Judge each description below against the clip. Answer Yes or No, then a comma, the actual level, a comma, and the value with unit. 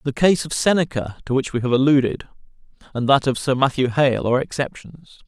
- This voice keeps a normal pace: Yes, average, 195 wpm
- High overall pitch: No, low, 135 Hz